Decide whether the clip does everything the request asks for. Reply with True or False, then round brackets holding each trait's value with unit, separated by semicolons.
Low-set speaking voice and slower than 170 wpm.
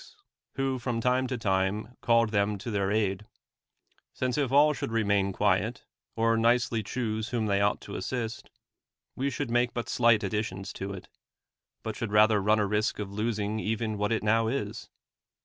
False (110 Hz; 185 wpm)